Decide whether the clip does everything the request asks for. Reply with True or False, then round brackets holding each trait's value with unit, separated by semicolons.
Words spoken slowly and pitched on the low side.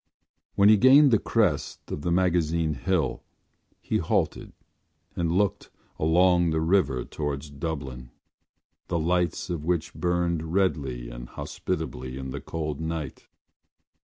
True (130 wpm; 80 Hz)